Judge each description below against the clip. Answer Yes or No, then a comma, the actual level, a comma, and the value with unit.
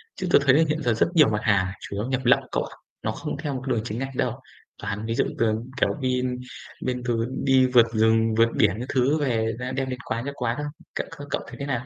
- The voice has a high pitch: No, low, 125 Hz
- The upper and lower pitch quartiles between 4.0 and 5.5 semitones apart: No, average, 3.0 semitones